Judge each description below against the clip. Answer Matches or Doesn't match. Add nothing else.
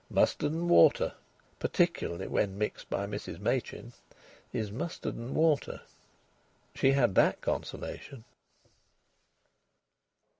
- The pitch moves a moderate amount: Doesn't match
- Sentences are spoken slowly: Matches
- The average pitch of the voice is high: Doesn't match